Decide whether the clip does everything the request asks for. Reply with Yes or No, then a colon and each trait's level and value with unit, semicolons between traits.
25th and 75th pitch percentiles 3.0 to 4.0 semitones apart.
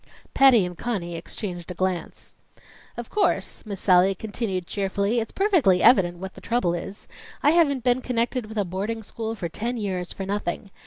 No: average, 4.5 semitones